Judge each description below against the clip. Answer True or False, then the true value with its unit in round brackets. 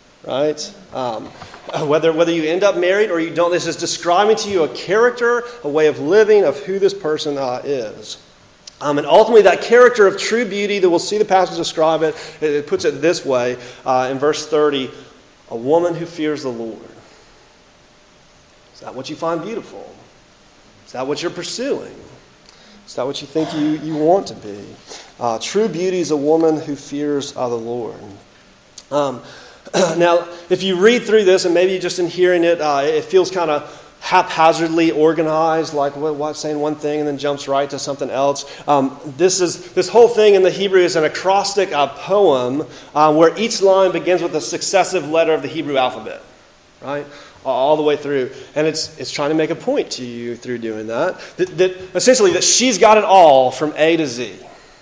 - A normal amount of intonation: True (4.1 semitones)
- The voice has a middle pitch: True (160 Hz)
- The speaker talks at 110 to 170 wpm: False (195 wpm)